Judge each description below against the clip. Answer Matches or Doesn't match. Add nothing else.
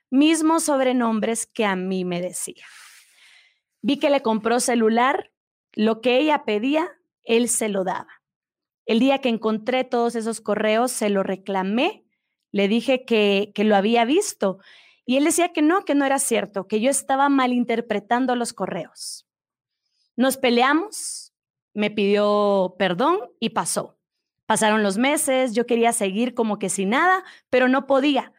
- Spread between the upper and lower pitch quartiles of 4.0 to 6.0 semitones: Matches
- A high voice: Matches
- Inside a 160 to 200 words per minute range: Doesn't match